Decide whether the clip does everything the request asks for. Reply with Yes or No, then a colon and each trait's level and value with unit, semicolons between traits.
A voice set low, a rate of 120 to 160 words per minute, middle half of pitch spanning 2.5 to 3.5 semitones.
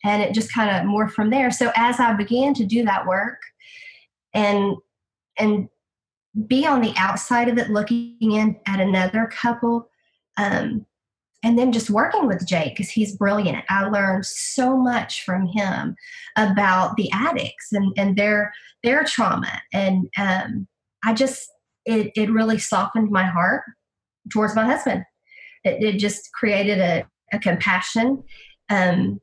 No: high, 215 Hz; average, 150 wpm; average, 3.2 semitones